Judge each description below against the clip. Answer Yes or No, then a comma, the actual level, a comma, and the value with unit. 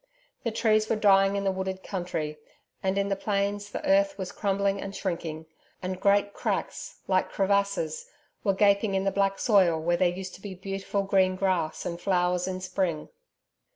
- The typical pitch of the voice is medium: No, high, 195 Hz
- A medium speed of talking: Yes, average, 180 wpm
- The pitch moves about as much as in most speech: No, narrow, 1.6 semitones